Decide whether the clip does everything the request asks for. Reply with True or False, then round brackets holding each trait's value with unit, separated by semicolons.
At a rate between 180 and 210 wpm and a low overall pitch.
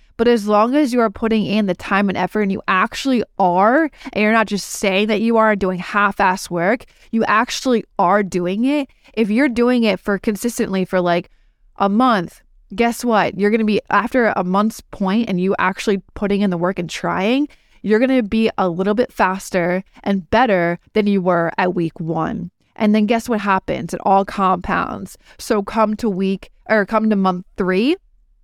False (200 wpm; 205 Hz)